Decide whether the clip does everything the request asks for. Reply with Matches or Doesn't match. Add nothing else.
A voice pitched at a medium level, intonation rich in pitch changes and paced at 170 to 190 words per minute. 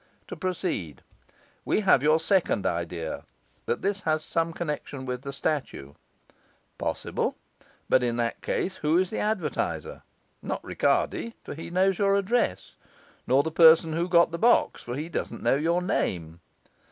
Doesn't match